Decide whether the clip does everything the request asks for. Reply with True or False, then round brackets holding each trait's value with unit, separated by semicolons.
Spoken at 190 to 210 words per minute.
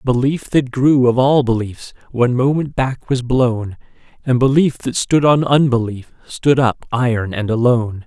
False (165 wpm)